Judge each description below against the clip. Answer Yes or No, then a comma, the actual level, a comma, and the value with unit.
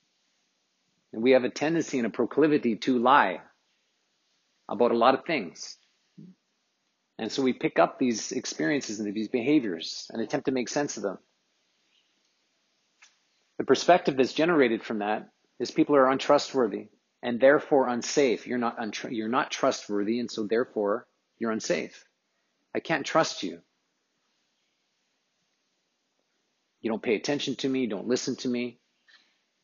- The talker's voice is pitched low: Yes, low, 130 Hz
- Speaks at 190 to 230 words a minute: No, average, 145 wpm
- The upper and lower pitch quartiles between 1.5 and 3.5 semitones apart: No, average, 4.1 semitones